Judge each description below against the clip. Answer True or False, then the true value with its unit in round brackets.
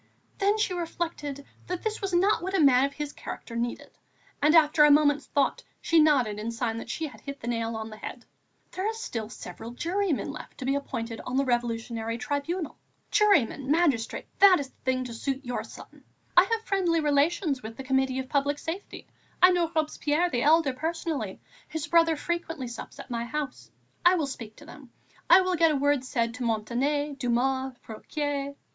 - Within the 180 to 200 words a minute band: True (195 wpm)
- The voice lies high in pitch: True (285 Hz)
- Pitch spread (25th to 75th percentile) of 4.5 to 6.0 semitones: True (5.1 semitones)